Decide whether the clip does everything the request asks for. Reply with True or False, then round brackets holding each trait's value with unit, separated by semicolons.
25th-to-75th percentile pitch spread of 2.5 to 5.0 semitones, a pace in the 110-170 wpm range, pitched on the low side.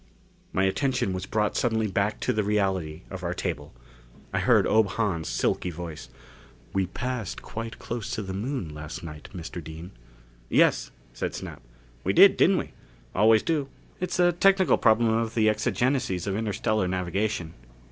True (4.1 semitones; 160 wpm; 105 Hz)